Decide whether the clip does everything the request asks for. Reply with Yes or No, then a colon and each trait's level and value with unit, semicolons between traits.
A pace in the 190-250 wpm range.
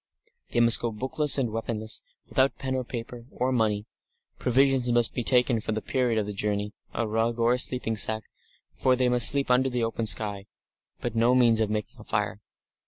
Yes: average, 195 wpm